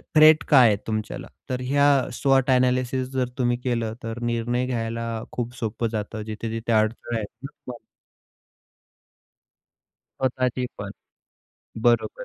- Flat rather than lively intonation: Yes, narrow, 2.1 semitones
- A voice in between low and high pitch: No, low, 120 Hz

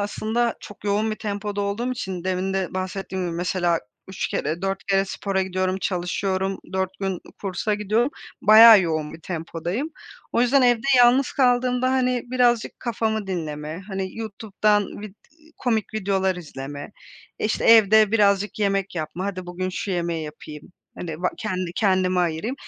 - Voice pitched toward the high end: Yes, high, 195 Hz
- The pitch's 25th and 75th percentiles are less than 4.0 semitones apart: Yes, average, 3.3 semitones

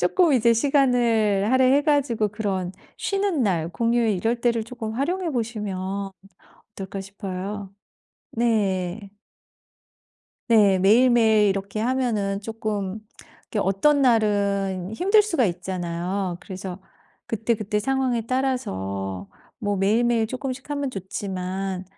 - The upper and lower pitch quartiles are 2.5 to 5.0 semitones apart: Yes, average, 4.2 semitones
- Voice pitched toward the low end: No, high, 215 Hz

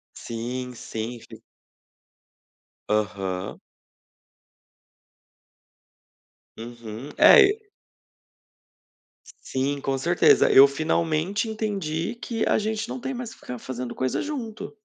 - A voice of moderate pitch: Yes, medium, 145 Hz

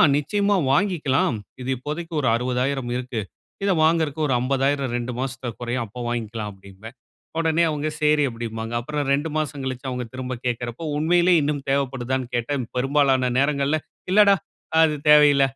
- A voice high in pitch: No, low, 135 Hz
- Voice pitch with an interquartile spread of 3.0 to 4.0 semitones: Yes, average, 3.4 semitones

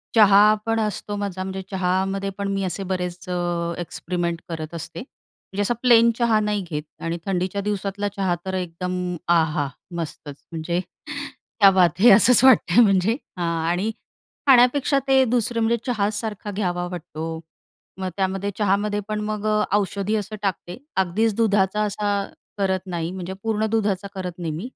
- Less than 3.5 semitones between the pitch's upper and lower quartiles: Yes, average, 3.1 semitones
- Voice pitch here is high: Yes, high, 195 Hz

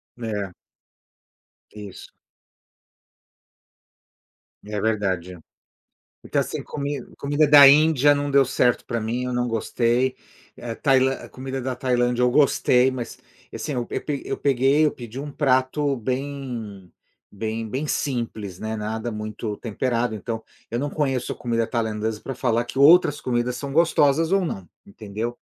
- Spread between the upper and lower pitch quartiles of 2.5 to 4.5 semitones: Yes, average, 3.7 semitones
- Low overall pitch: Yes, low, 125 Hz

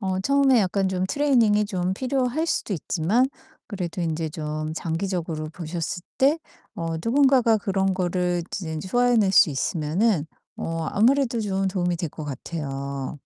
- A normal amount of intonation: No, wide, 5.7 semitones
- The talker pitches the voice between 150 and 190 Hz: Yes, medium, 185 Hz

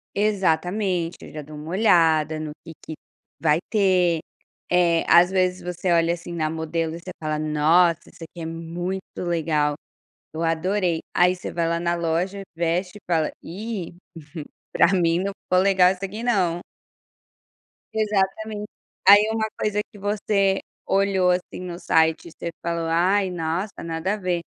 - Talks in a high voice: No, medium, 175 Hz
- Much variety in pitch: No, average, 2.7 semitones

